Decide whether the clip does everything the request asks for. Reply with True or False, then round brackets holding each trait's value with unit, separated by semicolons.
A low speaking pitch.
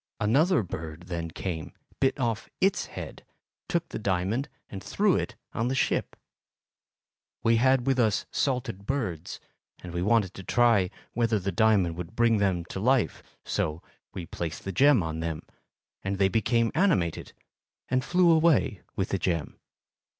True (110 Hz)